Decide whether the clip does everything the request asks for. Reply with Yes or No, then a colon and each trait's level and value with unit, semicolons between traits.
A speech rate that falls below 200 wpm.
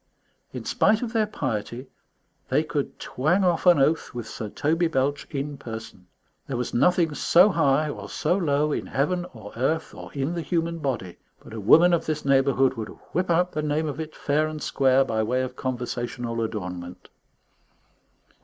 Yes: average, 180 wpm